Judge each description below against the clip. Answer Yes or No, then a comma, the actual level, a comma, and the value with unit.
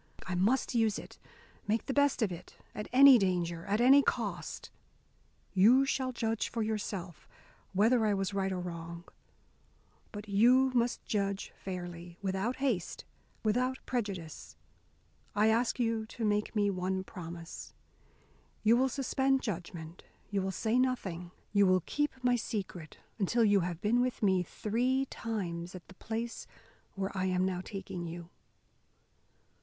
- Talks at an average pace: Yes, average, 150 wpm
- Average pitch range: Yes, average, 4.5 semitones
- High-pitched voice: Yes, high, 205 Hz